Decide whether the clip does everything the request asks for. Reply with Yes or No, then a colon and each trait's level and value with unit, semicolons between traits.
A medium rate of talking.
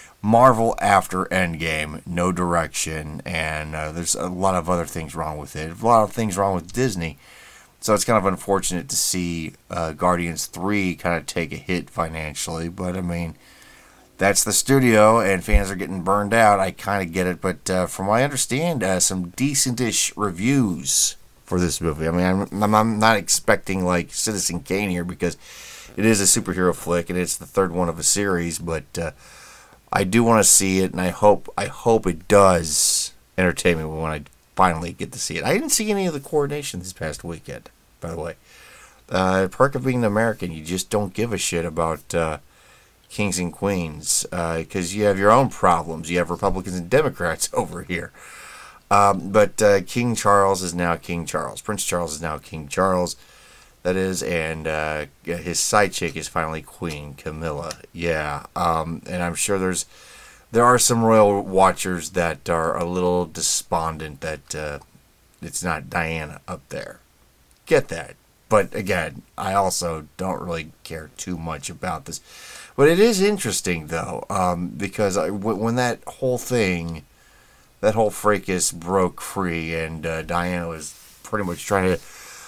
Yes: average, 180 wpm